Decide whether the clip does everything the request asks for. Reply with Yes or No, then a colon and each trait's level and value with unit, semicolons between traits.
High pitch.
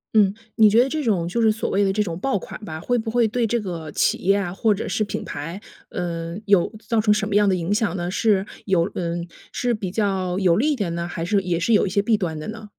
Yes: high, 200 Hz